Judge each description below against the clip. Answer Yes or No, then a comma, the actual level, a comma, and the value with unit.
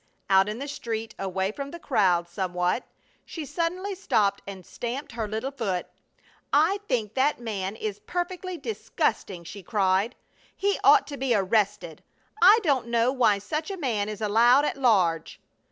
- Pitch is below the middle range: No, high, 225 Hz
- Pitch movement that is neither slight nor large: No, wide, 6.3 semitones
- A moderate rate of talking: Yes, average, 160 wpm